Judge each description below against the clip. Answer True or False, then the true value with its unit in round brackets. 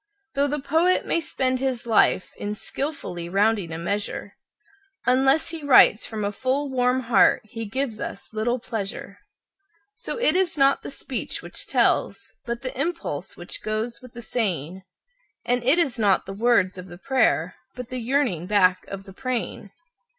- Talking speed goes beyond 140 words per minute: True (170 wpm)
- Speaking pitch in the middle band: False (235 Hz)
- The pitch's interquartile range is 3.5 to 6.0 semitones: True (5.1 semitones)